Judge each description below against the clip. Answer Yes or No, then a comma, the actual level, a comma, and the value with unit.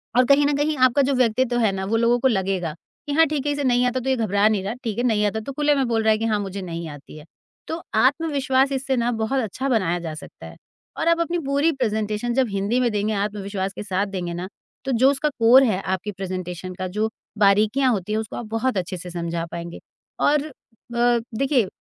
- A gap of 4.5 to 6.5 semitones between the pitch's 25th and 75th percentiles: Yes, average, 5.2 semitones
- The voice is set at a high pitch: Yes, high, 220 Hz